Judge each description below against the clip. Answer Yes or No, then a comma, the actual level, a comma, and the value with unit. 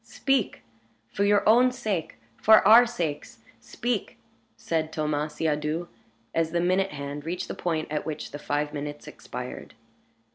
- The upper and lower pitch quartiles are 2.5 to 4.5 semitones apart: No, average, 5.3 semitones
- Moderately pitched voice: Yes, medium, 160 Hz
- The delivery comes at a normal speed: Yes, average, 145 wpm